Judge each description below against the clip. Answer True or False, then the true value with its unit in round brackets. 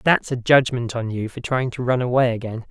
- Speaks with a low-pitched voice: True (120 Hz)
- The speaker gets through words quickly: True (245 wpm)